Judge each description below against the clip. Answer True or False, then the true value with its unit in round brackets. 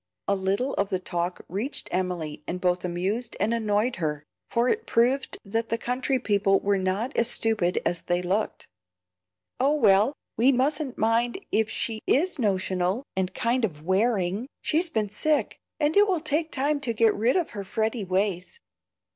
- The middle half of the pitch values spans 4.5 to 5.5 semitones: True (5.2 semitones)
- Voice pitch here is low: False (220 Hz)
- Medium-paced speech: True (170 wpm)